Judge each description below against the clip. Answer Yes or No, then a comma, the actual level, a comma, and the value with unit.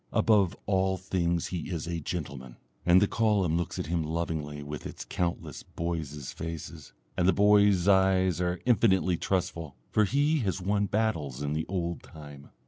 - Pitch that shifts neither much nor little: Yes, average, 3.3 semitones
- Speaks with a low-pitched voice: Yes, very low, 90 Hz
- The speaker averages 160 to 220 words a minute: Yes, average, 165 wpm